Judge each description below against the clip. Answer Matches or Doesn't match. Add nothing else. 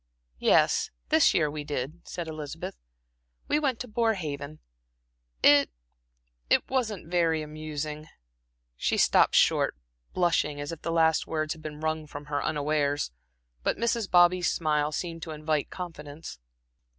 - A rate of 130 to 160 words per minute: Matches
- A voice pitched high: Doesn't match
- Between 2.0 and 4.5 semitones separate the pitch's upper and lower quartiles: Matches